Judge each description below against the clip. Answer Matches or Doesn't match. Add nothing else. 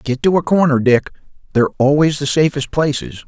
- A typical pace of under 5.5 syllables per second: Doesn't match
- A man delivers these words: Matches